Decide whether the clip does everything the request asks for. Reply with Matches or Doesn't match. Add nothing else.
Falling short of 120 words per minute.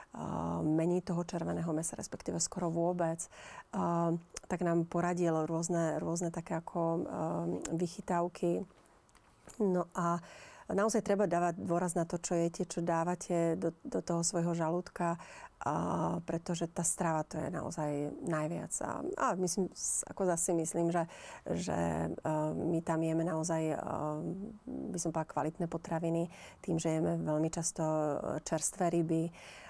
Doesn't match